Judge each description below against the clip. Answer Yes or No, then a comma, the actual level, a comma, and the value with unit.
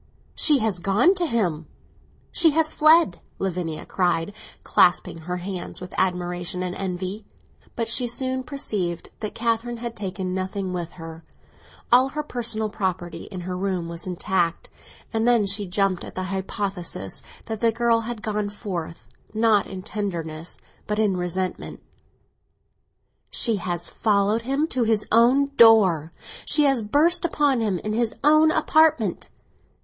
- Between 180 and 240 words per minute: No, average, 140 wpm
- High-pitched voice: Yes, high, 205 Hz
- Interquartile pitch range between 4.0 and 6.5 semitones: Yes, average, 4.6 semitones